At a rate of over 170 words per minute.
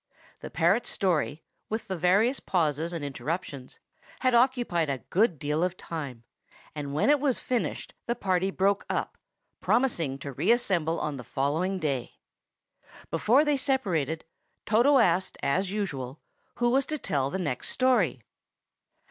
No: average, 145 wpm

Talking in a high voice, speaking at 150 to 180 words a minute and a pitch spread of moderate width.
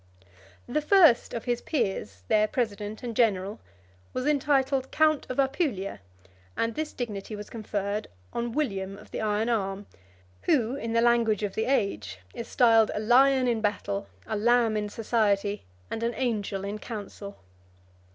Yes: high, 225 Hz; average, 155 wpm; average, 3.2 semitones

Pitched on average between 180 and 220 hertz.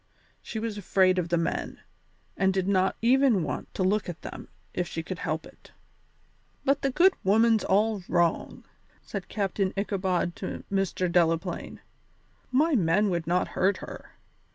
Yes: high, 190 Hz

